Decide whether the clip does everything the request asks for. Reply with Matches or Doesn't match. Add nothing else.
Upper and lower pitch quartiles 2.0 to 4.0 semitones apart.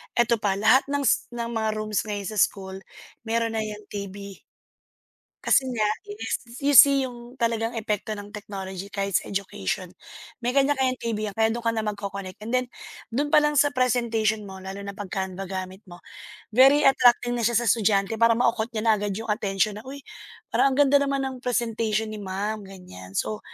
Matches